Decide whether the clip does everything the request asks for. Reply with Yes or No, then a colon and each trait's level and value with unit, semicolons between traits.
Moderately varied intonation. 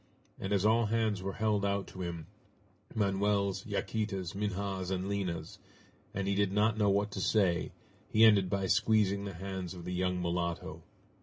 No: narrow, 1.9 semitones